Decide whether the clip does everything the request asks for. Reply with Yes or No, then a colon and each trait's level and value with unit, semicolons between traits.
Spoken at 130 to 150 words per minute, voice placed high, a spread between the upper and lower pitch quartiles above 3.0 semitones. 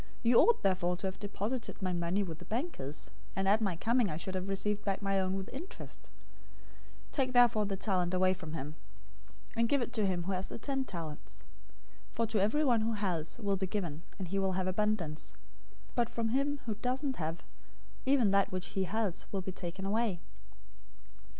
No: average, 200 wpm; high, 195 Hz; average, 3.8 semitones